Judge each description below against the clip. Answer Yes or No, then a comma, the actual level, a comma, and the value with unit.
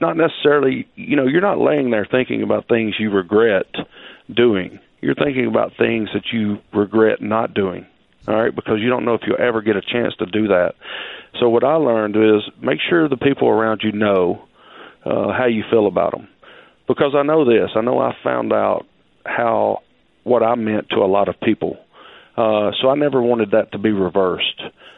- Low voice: Yes, low, 110 Hz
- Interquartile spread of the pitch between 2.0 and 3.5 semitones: Yes, average, 3.2 semitones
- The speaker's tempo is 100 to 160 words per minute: No, average, 200 wpm